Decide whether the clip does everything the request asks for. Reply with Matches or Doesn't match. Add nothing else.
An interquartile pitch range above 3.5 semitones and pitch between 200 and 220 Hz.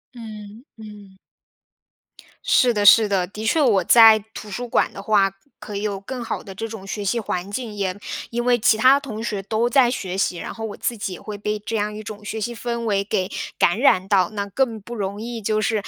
Doesn't match